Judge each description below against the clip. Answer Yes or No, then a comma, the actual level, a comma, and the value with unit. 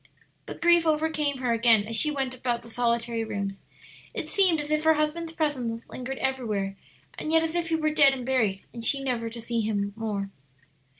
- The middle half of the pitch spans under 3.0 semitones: No, average, 5.1 semitones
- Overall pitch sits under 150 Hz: No, very high, 255 Hz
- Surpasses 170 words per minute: Yes, average, 200 wpm